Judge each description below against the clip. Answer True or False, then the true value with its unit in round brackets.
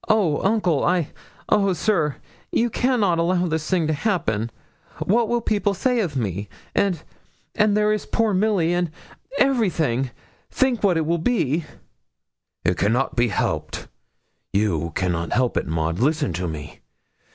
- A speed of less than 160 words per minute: True (145 wpm)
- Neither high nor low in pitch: True (170 Hz)